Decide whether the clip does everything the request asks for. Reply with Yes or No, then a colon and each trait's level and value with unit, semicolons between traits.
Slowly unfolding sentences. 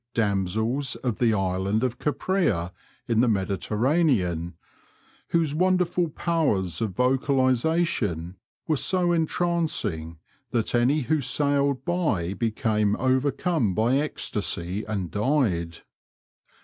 Yes: slow, 100 wpm